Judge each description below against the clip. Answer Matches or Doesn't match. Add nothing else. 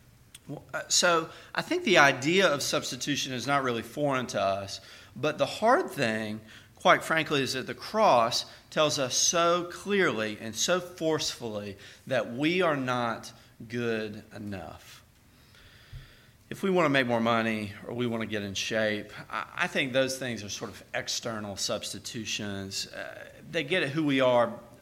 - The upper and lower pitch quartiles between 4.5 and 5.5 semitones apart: Matches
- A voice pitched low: Matches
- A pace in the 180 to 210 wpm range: Doesn't match